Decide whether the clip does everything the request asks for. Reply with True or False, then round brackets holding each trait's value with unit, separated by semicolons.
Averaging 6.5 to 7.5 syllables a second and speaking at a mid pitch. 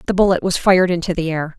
True (7.0 syllables/s; 180 Hz)